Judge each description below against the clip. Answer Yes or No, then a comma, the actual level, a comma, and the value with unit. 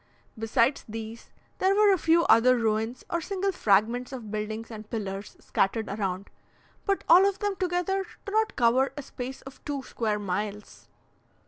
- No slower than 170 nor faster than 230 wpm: No, average, 160 wpm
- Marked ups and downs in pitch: Yes, wide, 7.9 semitones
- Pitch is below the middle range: No, high, 240 Hz